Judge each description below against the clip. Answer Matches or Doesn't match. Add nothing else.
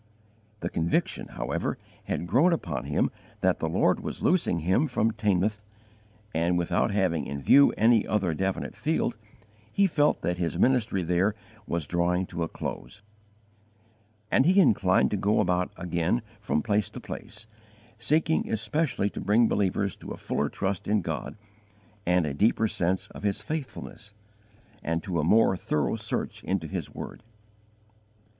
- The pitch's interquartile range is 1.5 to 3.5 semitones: Doesn't match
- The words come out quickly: Doesn't match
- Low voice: Matches